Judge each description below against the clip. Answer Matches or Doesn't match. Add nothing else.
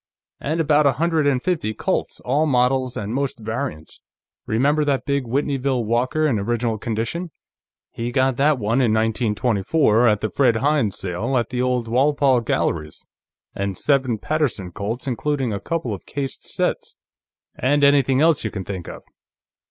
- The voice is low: Matches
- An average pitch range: Matches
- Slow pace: Doesn't match